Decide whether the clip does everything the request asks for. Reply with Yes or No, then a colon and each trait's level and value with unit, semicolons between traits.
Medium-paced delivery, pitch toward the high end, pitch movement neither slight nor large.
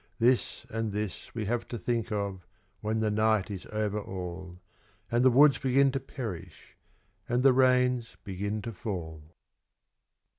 No: average, 150 wpm; low, 110 Hz; average, 3.8 semitones